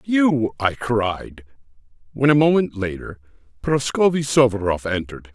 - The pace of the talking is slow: Yes, slow, 110 wpm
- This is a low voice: Yes, low, 120 Hz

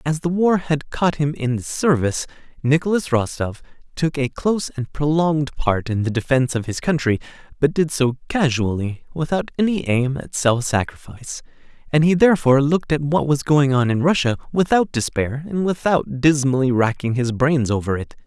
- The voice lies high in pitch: No, medium, 140 Hz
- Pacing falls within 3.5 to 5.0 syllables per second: No, 5.3 syllables/s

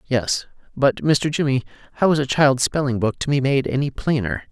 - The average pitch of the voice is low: Yes, low, 130 Hz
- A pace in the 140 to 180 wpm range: No, average, 200 wpm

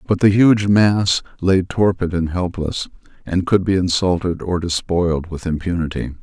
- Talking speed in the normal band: Yes, average, 155 wpm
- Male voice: Yes, male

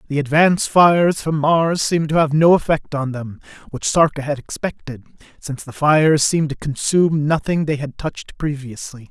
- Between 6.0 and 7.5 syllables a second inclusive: No, 5.4 syllables/s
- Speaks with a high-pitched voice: No, medium, 150 Hz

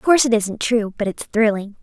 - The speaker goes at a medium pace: No, fast, 265 wpm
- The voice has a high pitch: Yes, high, 225 Hz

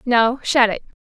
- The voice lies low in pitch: No, high, 235 Hz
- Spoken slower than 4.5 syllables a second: Yes, 4.1 syllables/s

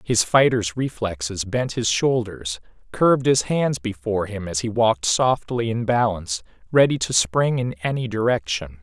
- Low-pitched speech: Yes, low, 110 Hz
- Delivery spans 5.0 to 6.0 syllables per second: No, 4.7 syllables/s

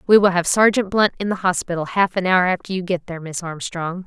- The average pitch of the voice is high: No, medium, 180 Hz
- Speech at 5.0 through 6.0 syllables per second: Yes, 5.9 syllables/s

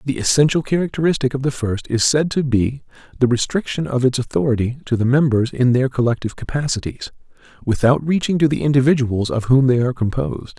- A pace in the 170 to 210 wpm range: Yes, average, 180 wpm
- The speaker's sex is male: Yes, male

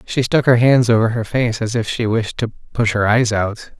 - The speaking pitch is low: Yes, low, 115 Hz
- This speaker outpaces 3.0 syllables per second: Yes, 5.0 syllables/s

